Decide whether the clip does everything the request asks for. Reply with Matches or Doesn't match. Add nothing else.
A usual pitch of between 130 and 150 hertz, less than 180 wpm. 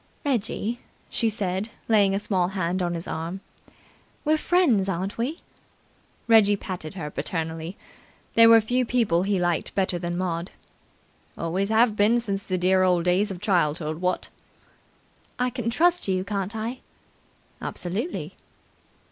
Doesn't match